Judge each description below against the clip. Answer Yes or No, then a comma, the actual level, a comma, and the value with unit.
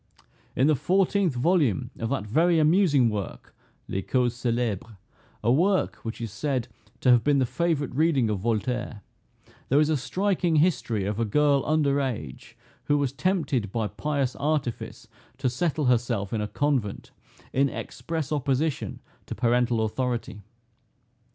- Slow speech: No, average, 150 wpm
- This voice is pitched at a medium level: No, low, 130 Hz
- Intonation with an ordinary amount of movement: Yes, average, 4.8 semitones